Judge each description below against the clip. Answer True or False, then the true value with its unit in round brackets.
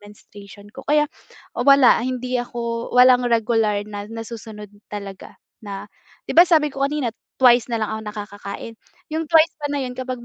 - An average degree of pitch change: True (3.7 semitones)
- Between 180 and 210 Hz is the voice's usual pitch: False (235 Hz)